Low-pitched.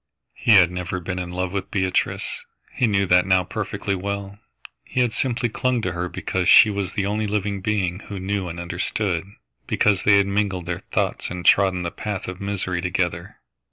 Yes: very low, 95 Hz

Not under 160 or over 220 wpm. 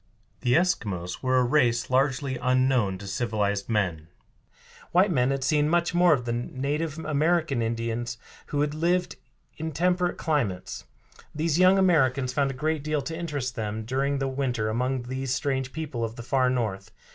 Yes: average, 170 wpm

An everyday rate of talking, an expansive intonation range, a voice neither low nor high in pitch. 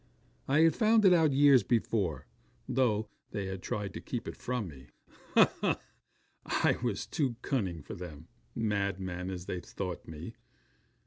No: average, 155 wpm; wide, 6.3 semitones; low, 105 Hz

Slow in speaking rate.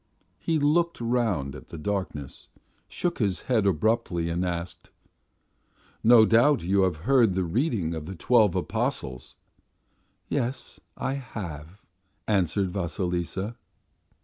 Yes: slow, 120 wpm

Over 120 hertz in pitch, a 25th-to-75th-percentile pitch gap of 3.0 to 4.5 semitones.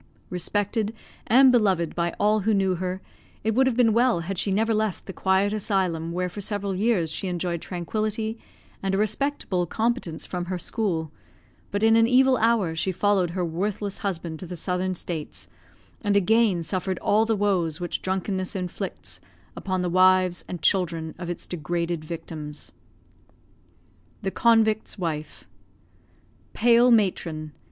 Yes: high, 190 Hz; average, 3.7 semitones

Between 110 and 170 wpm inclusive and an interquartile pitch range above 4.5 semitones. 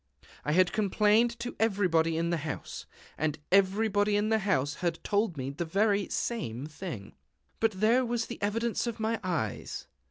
Yes: average, 165 wpm; average, 5.2 semitones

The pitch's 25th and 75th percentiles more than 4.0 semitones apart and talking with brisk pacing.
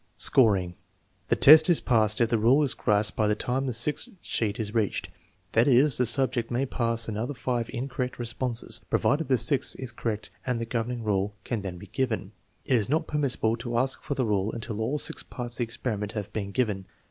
No: average, 3.2 semitones; fast, 210 wpm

